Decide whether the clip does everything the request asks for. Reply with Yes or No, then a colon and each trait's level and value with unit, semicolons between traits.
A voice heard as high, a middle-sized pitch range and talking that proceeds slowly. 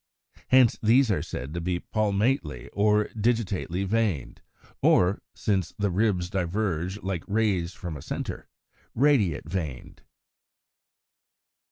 No: low, 100 Hz; average, 3.9 semitones; slow, 115 wpm